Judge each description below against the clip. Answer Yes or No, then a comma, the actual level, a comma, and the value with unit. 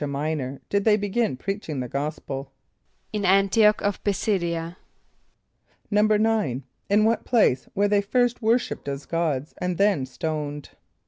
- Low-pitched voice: No, medium, 185 Hz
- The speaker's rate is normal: Yes, average, 150 wpm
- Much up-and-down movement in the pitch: Yes, wide, 6.1 semitones